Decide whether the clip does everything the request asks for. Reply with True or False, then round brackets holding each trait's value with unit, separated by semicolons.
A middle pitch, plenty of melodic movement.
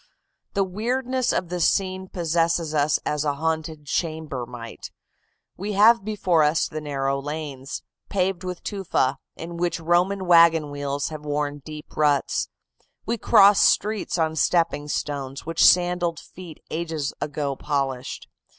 False (160 Hz; 3.8 semitones)